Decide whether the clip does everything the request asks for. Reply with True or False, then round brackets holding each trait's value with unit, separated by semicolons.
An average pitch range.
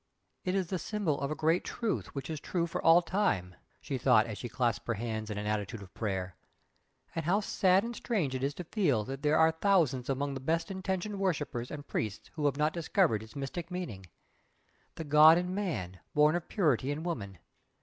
False (6.9 semitones)